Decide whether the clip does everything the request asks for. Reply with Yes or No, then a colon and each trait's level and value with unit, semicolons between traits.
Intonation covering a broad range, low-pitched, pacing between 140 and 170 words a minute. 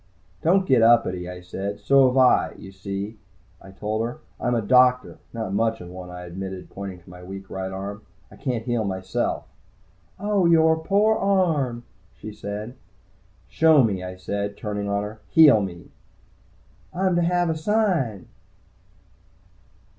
Yes: wide, 7.4 semitones; low, 110 Hz; average, 160 wpm